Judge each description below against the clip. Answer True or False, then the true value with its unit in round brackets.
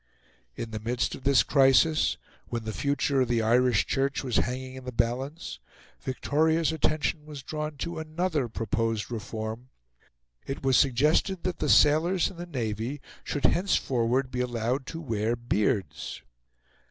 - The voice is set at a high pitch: False (130 Hz)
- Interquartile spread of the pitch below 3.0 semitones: False (4.5 semitones)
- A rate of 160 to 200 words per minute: False (150 wpm)